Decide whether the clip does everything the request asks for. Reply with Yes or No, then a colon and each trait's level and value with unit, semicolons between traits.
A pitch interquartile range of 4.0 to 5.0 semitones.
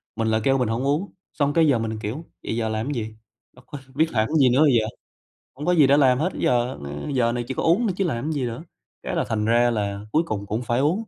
Yes: average, 4.6 semitones